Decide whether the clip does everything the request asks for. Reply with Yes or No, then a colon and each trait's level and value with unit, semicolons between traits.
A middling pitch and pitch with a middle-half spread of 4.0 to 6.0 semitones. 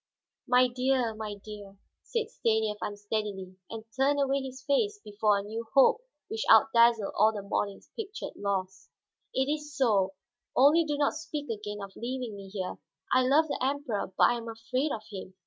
No: high, 230 Hz; average, 5.1 semitones